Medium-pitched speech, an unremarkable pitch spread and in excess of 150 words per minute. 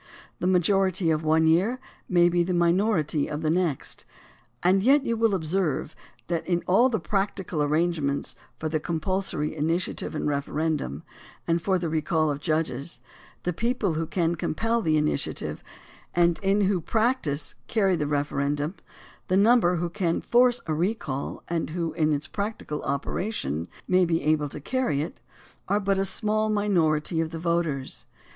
Yes: medium, 170 Hz; average, 4.1 semitones; average, 160 wpm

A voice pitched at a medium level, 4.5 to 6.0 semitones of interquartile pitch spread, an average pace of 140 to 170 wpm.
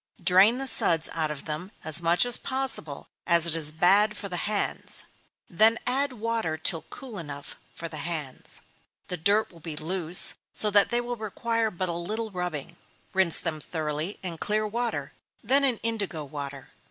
No: medium, 180 Hz; wide, 5.5 semitones; average, 180 wpm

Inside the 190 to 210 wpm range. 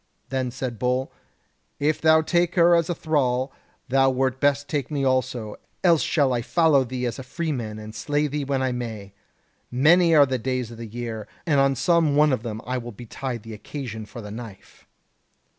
Yes: average, 195 wpm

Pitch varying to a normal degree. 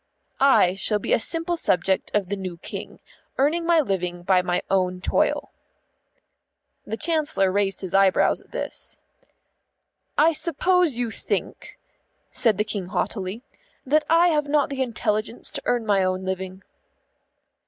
No: wide, 7.6 semitones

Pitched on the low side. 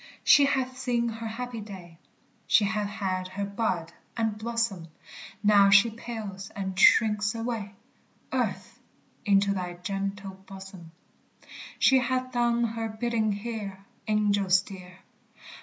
No: high, 210 Hz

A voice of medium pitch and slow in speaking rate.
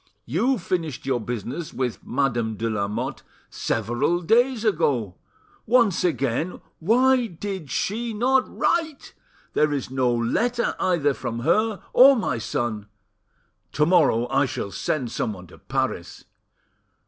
Yes: medium, 150 Hz; slow, 125 wpm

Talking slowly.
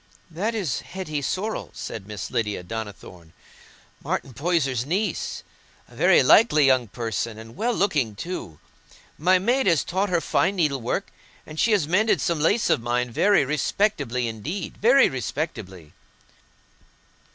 Yes: slow, 130 wpm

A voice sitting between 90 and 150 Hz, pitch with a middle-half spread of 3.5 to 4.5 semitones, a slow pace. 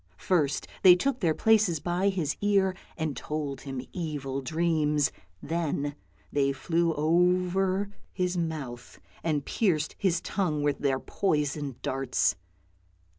No: medium, 160 Hz; average, 4.0 semitones; slow, 125 wpm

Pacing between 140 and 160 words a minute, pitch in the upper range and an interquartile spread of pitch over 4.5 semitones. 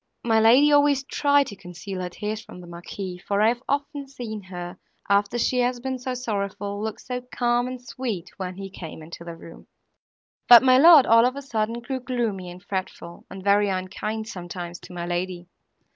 No: average, 195 wpm; high, 215 Hz; average, 5.2 semitones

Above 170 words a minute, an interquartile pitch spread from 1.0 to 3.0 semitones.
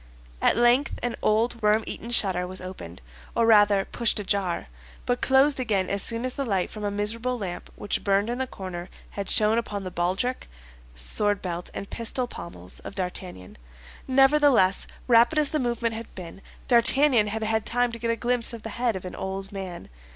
No: average, 190 wpm; average, 3.9 semitones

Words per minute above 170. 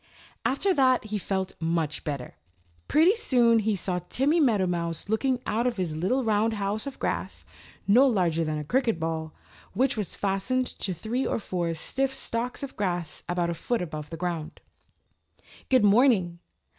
No: average, 165 wpm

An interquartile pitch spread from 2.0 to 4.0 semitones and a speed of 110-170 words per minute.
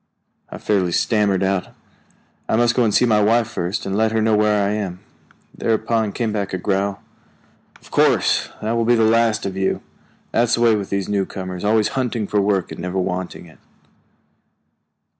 No: average, 2.7 semitones; average, 185 wpm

